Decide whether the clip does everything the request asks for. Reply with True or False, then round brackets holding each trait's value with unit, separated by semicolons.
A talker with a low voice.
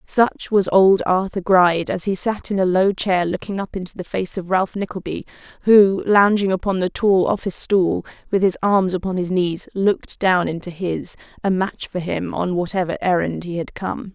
False (185 Hz)